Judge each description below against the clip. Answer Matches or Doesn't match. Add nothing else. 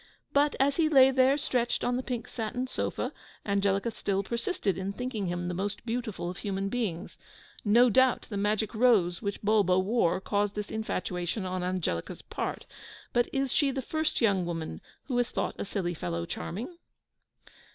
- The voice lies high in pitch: Matches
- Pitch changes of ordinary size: Matches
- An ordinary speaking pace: Matches